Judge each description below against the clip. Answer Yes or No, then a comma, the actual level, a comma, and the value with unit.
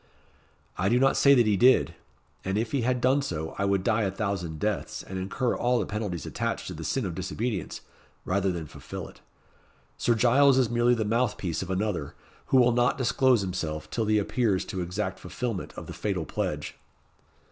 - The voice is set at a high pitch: No, low, 105 Hz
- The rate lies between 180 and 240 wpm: Yes, average, 200 wpm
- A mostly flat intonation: No, average, 4.6 semitones